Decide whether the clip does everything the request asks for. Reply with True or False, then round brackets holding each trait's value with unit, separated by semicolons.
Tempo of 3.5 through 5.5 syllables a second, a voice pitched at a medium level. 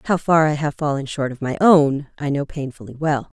True (5.3 syllables/s; 145 Hz)